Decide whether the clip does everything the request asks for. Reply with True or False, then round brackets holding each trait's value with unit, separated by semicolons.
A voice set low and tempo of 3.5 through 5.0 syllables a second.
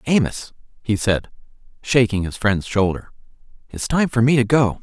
True (115 Hz; 4.9 syllables/s)